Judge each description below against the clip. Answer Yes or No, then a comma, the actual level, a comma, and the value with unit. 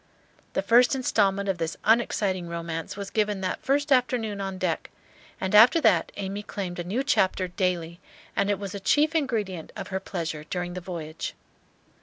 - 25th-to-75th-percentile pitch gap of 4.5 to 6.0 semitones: No, average, 3.6 semitones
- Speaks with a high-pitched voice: Yes, high, 195 Hz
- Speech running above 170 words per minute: Yes, average, 180 wpm